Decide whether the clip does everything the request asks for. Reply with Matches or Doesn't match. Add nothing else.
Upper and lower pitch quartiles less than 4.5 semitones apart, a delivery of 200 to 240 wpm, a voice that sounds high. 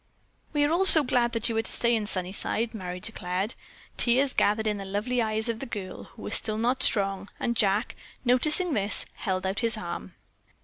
Matches